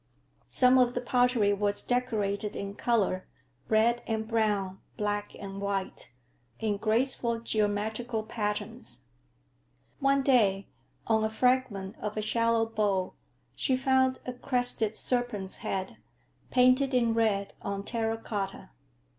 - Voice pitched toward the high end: Yes, high, 220 Hz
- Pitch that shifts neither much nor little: Yes, average, 3.3 semitones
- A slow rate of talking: Yes, slow, 120 wpm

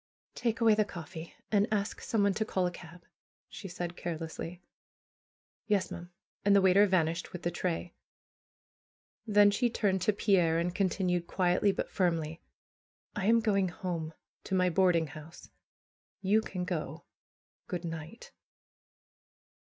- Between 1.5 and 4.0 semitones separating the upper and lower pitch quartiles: Yes, average, 3.0 semitones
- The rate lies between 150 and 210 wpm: No, average, 140 wpm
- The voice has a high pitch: No, medium, 180 Hz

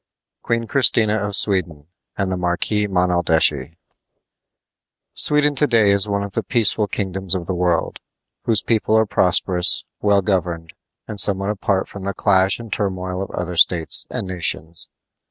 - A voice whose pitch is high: No, very low, 95 Hz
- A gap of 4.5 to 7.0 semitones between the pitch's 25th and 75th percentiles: No, average, 2.8 semitones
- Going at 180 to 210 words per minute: No, average, 155 wpm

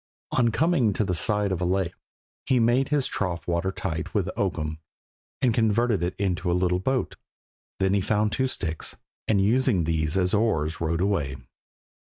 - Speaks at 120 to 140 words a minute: No, average, 175 wpm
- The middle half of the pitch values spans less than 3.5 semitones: No, average, 4.4 semitones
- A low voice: Yes, very low, 95 Hz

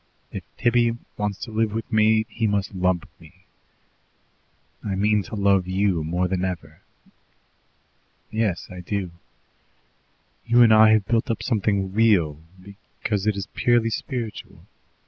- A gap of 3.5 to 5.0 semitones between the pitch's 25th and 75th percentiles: No, average, 3.1 semitones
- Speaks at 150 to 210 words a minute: No, average, 140 wpm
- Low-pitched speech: Yes, low, 105 Hz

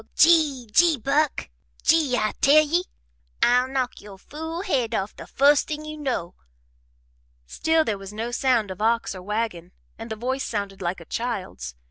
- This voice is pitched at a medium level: No, high, 245 Hz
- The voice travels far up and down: Yes, wide, 6.2 semitones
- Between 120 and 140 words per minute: No, average, 170 wpm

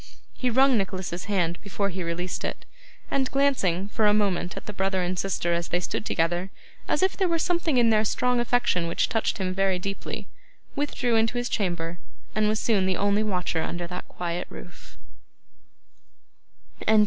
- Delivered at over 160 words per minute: Yes, average, 175 wpm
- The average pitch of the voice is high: Yes, high, 195 Hz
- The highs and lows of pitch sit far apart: No, average, 4.7 semitones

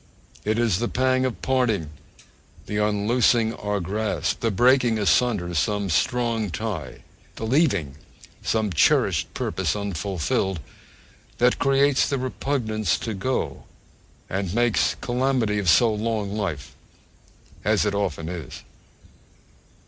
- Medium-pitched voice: No, low, 110 Hz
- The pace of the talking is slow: Yes, slow, 120 wpm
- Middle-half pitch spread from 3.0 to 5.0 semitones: Yes, average, 4.1 semitones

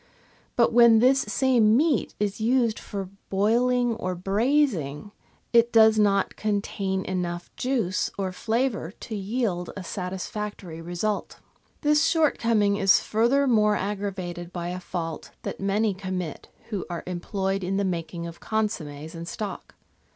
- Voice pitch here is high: Yes, high, 200 Hz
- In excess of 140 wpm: No, slow, 135 wpm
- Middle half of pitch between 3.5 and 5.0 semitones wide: Yes, average, 4.0 semitones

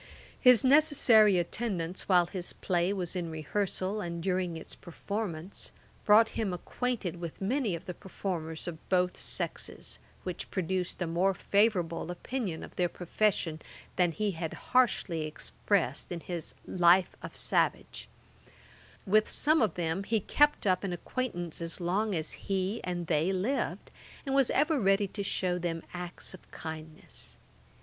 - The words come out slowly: No, average, 150 wpm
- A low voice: No, medium, 185 Hz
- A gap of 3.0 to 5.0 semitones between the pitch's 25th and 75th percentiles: Yes, average, 3.5 semitones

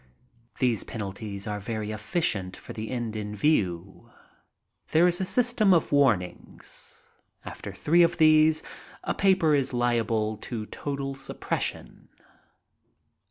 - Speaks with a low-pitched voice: Yes, low, 120 Hz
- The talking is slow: Yes, slow, 120 wpm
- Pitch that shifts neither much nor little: No, wide, 6.8 semitones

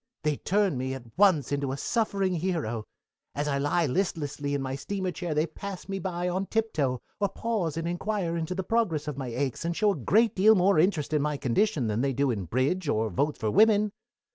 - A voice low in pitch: No, medium, 160 Hz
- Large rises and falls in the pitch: Yes, wide, 5.7 semitones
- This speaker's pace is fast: Yes, fast, 220 wpm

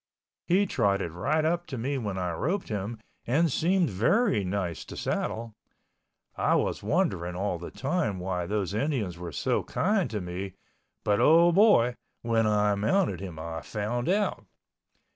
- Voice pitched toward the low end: Yes, low, 110 Hz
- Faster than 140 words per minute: Yes, average, 160 wpm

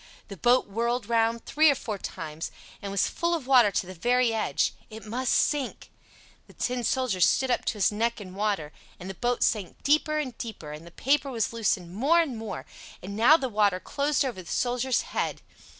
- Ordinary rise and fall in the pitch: Yes, average, 4.5 semitones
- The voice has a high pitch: Yes, high, 230 Hz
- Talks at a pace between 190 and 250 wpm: Yes, average, 200 wpm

